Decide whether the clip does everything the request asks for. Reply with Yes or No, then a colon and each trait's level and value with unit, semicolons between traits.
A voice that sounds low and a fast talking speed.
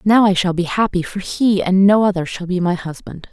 No: medium, 185 Hz; fast, 255 wpm